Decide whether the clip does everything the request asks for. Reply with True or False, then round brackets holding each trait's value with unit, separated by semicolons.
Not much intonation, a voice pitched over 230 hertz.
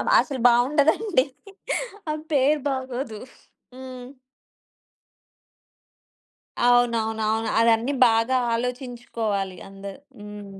False (3.0 semitones; 245 Hz)